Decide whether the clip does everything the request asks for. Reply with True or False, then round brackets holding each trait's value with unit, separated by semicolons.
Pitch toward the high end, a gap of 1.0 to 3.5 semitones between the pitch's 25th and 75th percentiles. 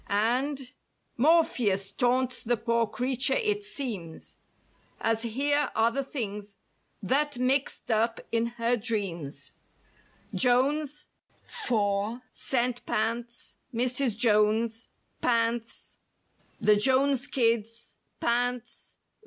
True (235 Hz; 2.9 semitones)